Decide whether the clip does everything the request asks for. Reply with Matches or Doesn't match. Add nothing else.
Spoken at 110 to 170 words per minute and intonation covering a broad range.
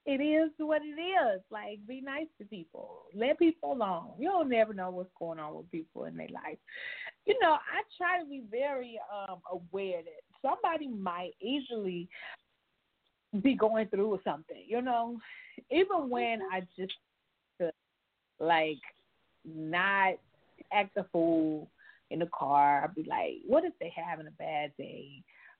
Matches